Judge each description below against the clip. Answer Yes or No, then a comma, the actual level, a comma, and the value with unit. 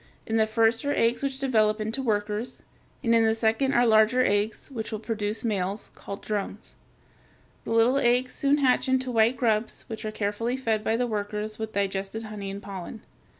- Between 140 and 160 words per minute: No, average, 190 wpm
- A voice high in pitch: Yes, high, 220 Hz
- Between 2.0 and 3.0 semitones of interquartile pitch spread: Yes, narrow, 2.4 semitones